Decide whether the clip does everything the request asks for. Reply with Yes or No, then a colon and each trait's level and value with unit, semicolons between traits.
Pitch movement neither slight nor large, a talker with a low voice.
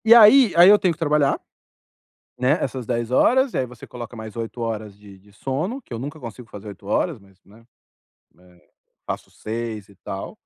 No: wide, 6.6 semitones; low, 120 Hz